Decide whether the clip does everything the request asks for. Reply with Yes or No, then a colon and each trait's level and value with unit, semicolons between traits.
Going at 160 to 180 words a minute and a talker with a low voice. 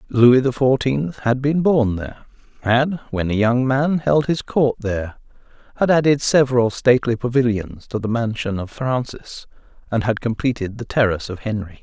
Yes: average, 165 wpm; low, 120 Hz